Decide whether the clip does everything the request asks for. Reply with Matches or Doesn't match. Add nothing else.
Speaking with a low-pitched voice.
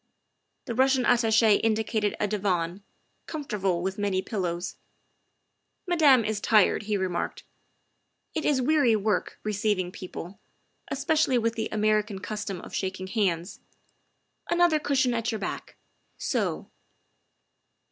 Doesn't match